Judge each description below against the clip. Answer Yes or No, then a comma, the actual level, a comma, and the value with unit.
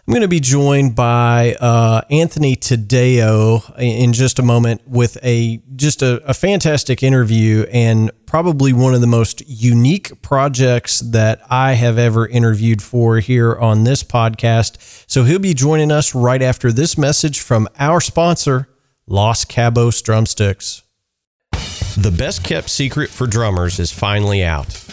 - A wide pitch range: No, average, 3.1 semitones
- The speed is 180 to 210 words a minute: No, average, 150 wpm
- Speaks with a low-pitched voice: Yes, low, 120 Hz